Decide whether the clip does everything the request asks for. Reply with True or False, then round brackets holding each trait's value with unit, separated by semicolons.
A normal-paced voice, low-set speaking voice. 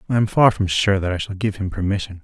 False (295 wpm; 100 Hz)